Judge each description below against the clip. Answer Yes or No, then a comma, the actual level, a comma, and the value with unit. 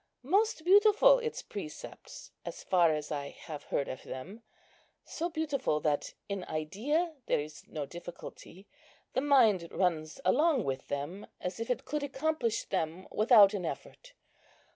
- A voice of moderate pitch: No, high, 205 Hz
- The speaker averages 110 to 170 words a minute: Yes, average, 145 wpm